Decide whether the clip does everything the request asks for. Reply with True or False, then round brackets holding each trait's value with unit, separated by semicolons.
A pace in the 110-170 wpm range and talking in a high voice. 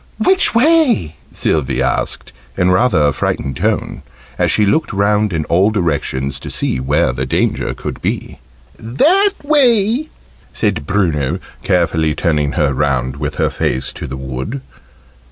False (145 wpm; 85 Hz)